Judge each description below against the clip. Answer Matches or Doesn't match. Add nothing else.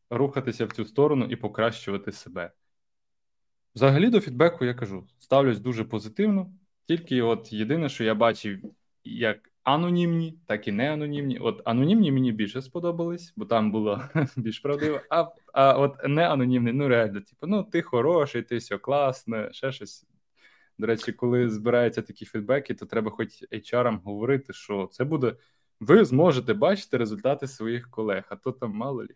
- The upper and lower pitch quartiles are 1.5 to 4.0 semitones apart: Doesn't match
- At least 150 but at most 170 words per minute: Matches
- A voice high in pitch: Doesn't match